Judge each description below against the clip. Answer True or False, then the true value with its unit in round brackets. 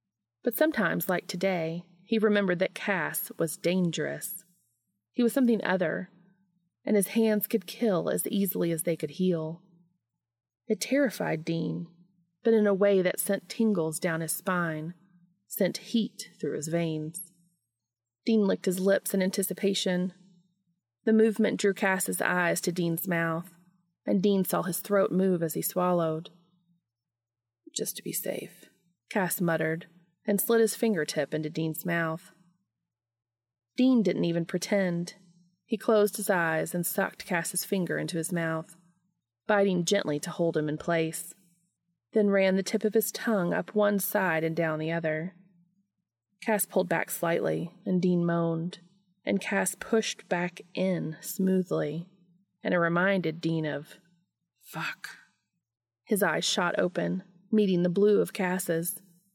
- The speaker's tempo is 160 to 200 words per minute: False (145 wpm)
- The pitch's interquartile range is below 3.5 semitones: True (2.9 semitones)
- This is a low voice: False (180 Hz)